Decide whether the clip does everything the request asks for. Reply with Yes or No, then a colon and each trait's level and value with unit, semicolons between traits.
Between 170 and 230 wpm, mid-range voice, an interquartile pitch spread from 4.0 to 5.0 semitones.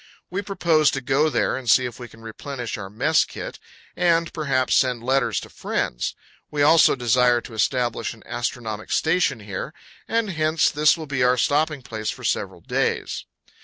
No: average, 175 wpm; low, 130 Hz; average, 4.6 semitones